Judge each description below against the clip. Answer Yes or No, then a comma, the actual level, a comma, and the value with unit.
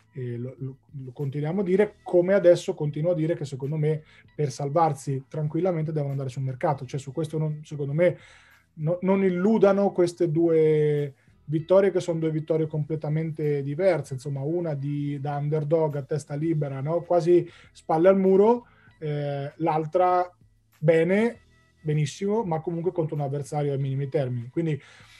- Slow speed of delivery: No, average, 155 wpm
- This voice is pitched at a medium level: Yes, medium, 155 Hz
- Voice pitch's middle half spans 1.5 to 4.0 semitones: Yes, average, 3.4 semitones